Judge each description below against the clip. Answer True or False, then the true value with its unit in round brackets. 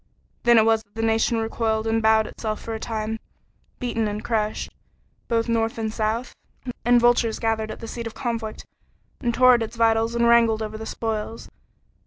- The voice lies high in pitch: True (225 Hz)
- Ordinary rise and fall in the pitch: False (1.1 semitones)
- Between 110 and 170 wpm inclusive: False (190 wpm)